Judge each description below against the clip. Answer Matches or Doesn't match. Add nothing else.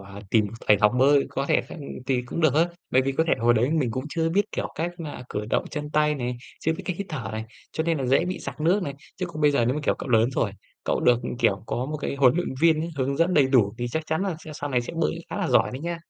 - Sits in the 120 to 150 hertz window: Matches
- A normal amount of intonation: Matches